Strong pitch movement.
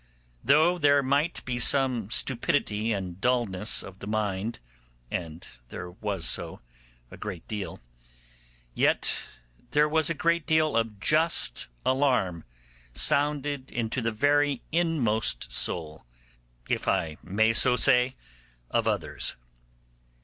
Yes: wide, 6.3 semitones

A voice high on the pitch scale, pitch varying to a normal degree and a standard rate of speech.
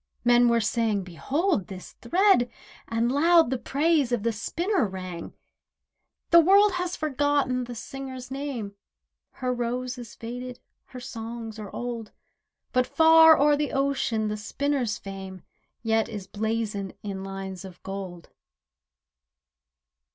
No: high, 240 Hz; average, 5.0 semitones; slow, 130 wpm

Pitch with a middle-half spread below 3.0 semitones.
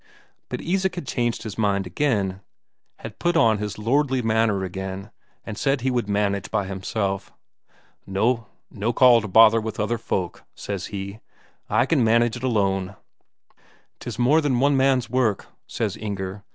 No: average, 4.2 semitones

